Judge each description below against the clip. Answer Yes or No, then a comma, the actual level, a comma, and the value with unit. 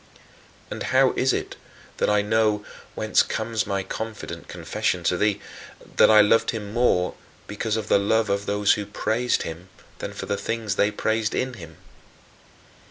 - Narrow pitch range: Yes, narrow, 2.1 semitones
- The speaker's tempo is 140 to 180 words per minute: Yes, average, 165 wpm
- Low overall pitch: Yes, low, 105 Hz